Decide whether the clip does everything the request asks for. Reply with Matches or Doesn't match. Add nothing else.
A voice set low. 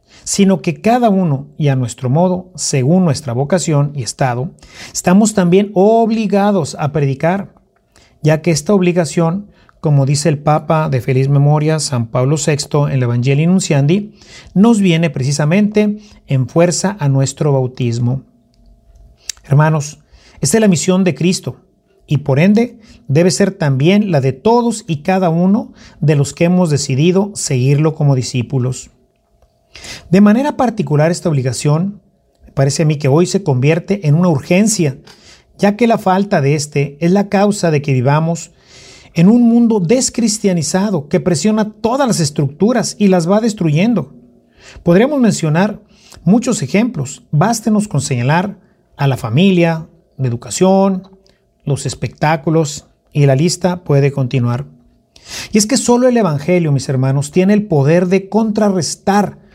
Doesn't match